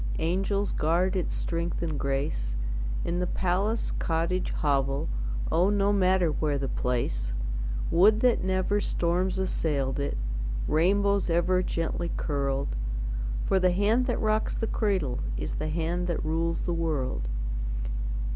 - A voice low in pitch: No, medium, 170 Hz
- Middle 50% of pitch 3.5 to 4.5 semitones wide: Yes, average, 4.2 semitones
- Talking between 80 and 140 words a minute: Yes, slow, 135 wpm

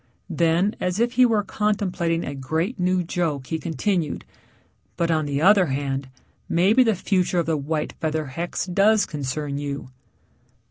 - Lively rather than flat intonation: No, average, 4.7 semitones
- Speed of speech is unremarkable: Yes, average, 155 wpm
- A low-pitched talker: No, medium, 170 Hz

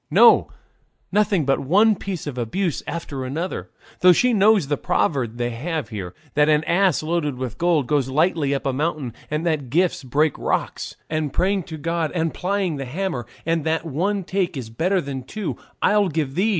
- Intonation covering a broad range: No, average, 5.0 semitones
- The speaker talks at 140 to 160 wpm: No, average, 190 wpm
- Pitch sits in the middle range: Yes, medium, 160 Hz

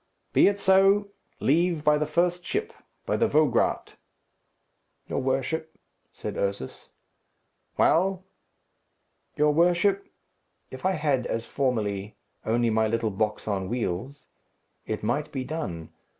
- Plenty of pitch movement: Yes, wide, 7.7 semitones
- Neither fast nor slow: No, slow, 120 wpm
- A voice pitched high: No, medium, 145 Hz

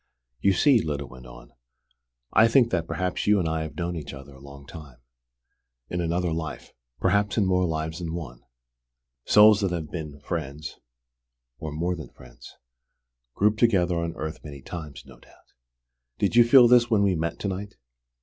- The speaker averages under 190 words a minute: Yes, average, 180 wpm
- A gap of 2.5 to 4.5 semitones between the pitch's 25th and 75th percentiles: No, average, 4.9 semitones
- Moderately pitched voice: No, very low, 85 Hz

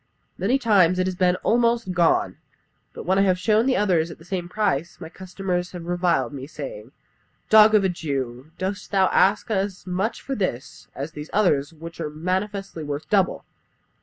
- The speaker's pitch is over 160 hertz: Yes, medium, 185 Hz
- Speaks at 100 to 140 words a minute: No, average, 190 wpm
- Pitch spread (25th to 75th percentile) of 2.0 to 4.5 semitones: Yes, average, 3.7 semitones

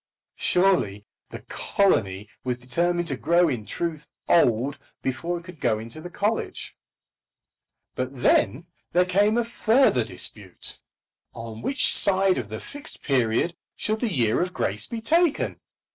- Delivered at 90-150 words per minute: Yes, average, 145 wpm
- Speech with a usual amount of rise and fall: No, wide, 8.8 semitones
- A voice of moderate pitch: Yes, medium, 165 Hz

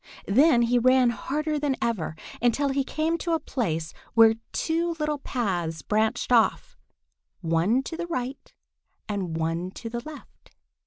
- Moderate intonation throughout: No, wide, 6.6 semitones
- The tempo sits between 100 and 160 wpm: Yes, average, 150 wpm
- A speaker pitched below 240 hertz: No, high, 245 Hz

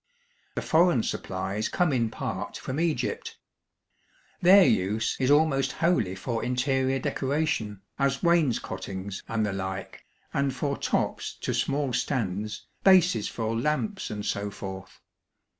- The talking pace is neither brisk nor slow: No, slow, 125 wpm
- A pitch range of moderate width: No, wide, 6.4 semitones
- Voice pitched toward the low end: Yes, low, 130 Hz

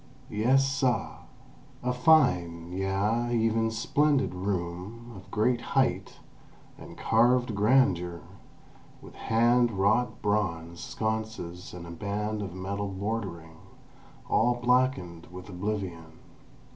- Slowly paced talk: Yes, slow, 105 wpm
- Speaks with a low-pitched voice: Yes, low, 105 Hz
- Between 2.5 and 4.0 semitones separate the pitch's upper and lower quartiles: No, average, 4.9 semitones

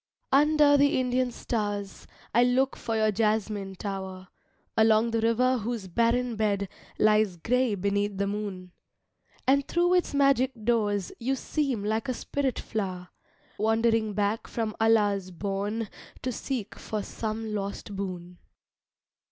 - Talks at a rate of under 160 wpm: Yes, slow, 135 wpm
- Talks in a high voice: Yes, high, 220 Hz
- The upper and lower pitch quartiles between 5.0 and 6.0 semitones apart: No, average, 3.6 semitones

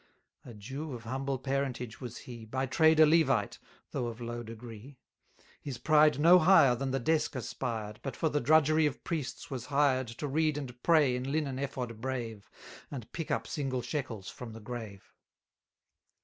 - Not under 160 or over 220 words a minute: Yes, average, 175 wpm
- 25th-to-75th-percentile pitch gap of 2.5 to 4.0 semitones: Yes, average, 3.7 semitones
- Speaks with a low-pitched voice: Yes, low, 130 Hz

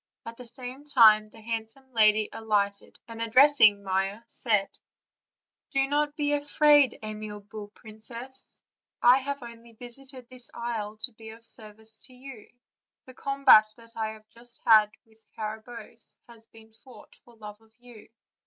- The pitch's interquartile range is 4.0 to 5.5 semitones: No, average, 2.9 semitones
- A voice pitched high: Yes, high, 230 Hz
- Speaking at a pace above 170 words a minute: No, average, 155 wpm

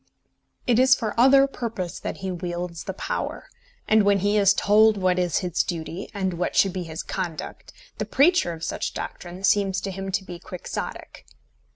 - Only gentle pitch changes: No, average, 3.2 semitones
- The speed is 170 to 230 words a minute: Yes, average, 185 wpm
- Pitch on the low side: No, high, 190 Hz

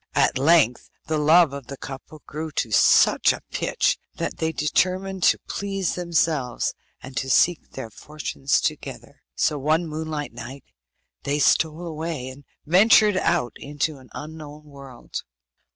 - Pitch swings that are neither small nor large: Yes, average, 3.3 semitones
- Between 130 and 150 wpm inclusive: Yes, average, 145 wpm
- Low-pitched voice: No, medium, 150 Hz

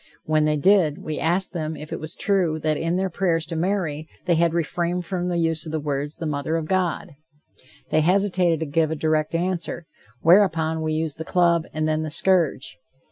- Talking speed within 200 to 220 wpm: Yes, fast, 205 wpm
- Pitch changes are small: Yes, narrow, 2.2 semitones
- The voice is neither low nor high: Yes, medium, 165 Hz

